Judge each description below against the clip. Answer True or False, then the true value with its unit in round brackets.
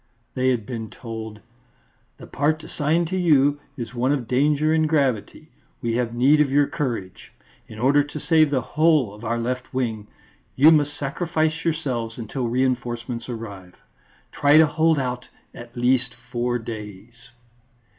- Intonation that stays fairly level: False (4.0 semitones)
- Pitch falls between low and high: False (130 Hz)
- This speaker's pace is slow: False (155 wpm)